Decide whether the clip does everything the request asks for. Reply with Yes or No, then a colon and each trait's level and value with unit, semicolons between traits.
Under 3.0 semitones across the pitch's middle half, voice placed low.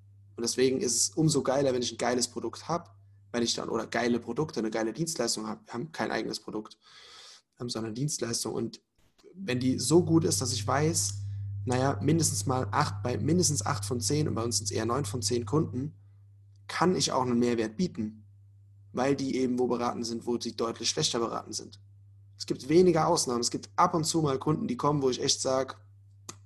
No: average, 4.3 semitones; low, 120 Hz